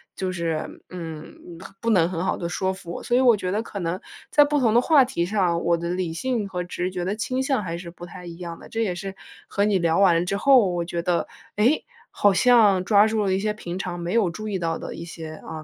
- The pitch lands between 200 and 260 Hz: No, medium, 185 Hz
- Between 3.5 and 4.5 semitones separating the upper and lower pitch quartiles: Yes, average, 3.8 semitones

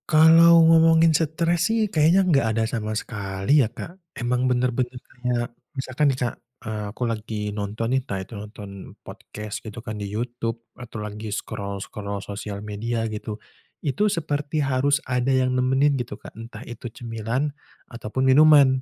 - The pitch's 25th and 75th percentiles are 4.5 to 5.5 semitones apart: Yes, average, 4.8 semitones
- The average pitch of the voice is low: Yes, low, 120 Hz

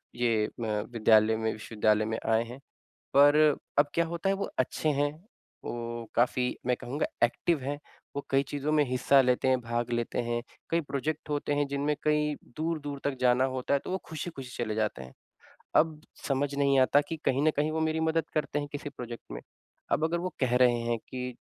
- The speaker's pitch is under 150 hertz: Yes, low, 135 Hz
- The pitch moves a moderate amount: Yes, average, 4.0 semitones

